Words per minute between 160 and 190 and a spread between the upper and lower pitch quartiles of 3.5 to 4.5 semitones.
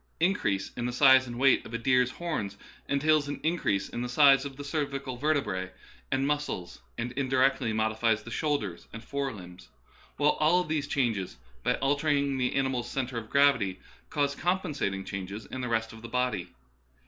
Yes: average, 175 wpm; average, 4.1 semitones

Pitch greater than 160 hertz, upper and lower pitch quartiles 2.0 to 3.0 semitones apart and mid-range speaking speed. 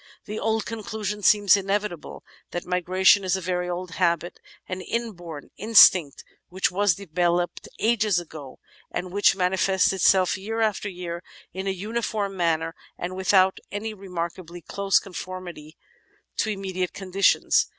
No: medium, 185 Hz; narrow, 2.4 semitones; slow, 130 wpm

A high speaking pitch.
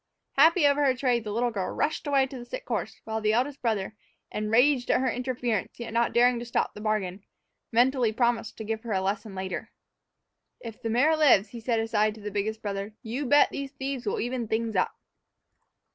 Yes: high, 235 Hz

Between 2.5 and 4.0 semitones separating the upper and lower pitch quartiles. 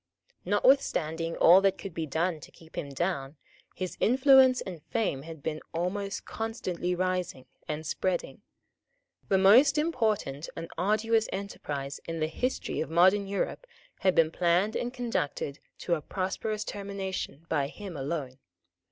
No: average, 4.5 semitones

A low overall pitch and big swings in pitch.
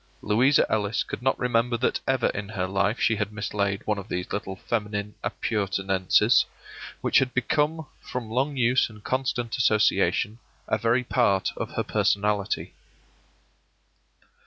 No: low, 110 Hz; average, 3.5 semitones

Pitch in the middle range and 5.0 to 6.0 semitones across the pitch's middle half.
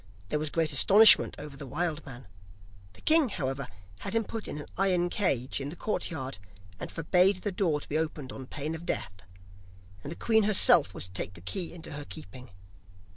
Yes: medium, 155 Hz; wide, 5.5 semitones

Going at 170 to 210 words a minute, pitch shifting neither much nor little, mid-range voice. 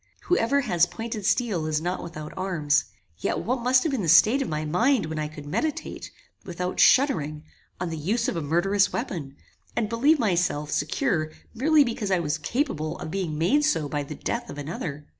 No: average, 195 wpm; wide, 7.3 semitones; medium, 180 Hz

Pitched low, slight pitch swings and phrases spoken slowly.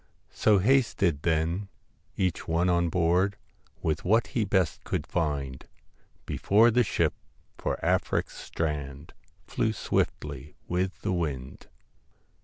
No: very low, 85 Hz; average, 4.7 semitones; slow, 120 wpm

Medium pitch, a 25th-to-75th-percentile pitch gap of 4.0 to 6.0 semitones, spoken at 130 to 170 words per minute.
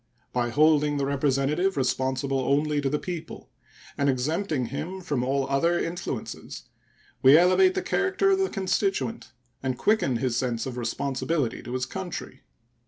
Yes: medium, 145 Hz; average, 5.1 semitones; average, 150 wpm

